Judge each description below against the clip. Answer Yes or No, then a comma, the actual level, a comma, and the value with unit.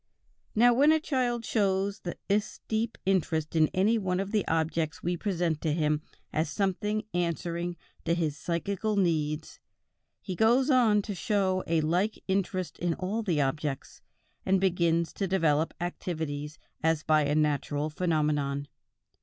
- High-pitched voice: No, medium, 175 Hz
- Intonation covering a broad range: No, average, 4.4 semitones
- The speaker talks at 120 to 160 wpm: Yes, average, 150 wpm